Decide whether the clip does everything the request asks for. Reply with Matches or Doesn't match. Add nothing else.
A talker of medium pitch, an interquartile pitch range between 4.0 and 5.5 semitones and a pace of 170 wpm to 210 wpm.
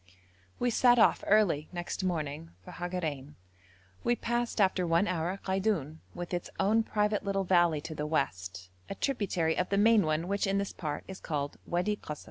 Matches